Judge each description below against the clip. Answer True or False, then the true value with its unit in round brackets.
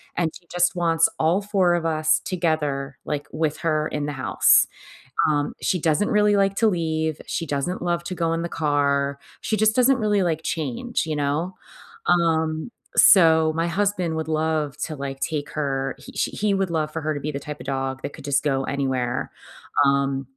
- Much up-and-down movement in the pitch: False (3.3 semitones)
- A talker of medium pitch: True (160 Hz)